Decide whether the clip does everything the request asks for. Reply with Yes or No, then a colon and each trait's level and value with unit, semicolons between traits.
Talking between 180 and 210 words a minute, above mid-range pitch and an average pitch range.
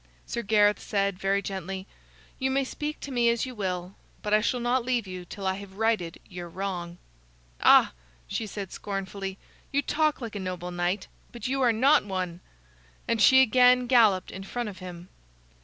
Yes: average, 185 wpm; high, 205 Hz; average, 4.4 semitones